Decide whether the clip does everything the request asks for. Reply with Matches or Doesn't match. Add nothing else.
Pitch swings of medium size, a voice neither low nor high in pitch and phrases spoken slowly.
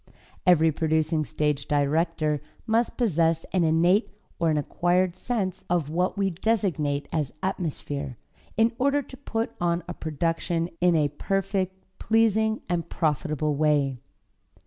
Matches